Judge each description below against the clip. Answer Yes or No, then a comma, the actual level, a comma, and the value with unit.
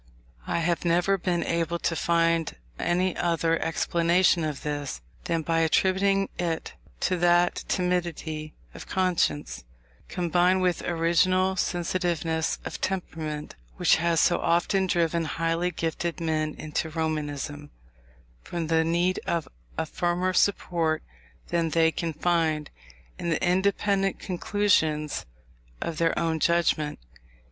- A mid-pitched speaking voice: Yes, medium, 170 Hz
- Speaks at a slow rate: Yes, slow, 120 wpm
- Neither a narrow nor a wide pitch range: No, narrow, 1.8 semitones